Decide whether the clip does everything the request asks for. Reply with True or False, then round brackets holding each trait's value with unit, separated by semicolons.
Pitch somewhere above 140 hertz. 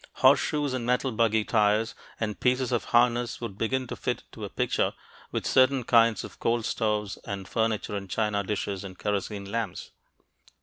False (110 Hz)